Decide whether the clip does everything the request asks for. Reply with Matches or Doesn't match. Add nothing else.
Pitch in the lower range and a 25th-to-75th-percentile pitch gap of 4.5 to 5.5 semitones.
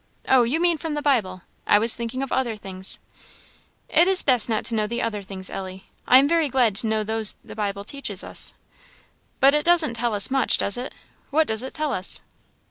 Doesn't match